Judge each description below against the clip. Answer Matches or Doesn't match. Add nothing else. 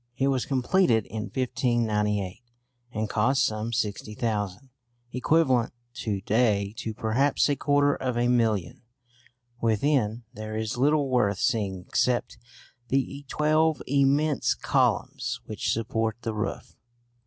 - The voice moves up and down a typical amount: Matches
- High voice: Doesn't match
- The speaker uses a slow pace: Matches